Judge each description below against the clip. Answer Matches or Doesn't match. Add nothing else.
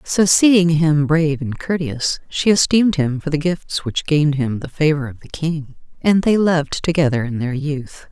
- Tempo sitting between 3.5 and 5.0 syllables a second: Matches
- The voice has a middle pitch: Matches